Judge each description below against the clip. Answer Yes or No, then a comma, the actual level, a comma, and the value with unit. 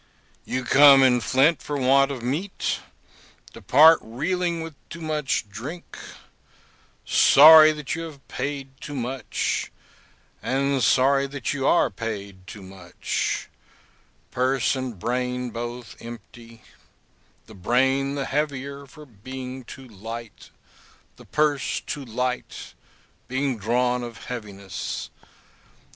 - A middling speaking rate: No, slow, 115 wpm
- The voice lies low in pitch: Yes, low, 130 Hz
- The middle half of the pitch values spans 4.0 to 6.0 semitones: No, average, 3.2 semitones